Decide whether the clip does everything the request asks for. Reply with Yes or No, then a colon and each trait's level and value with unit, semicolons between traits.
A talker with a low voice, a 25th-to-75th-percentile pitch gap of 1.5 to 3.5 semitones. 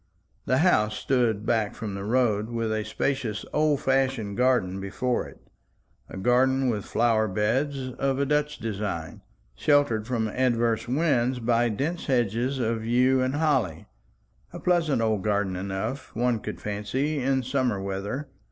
No: low, 120 Hz; average, 3.9 semitones